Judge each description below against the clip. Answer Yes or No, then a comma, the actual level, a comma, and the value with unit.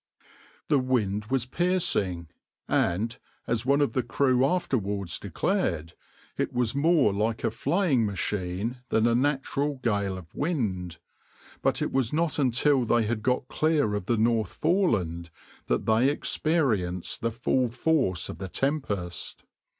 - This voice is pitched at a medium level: No, low, 120 Hz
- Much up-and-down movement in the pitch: Yes, wide, 5.7 semitones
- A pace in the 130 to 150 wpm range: Yes, average, 145 wpm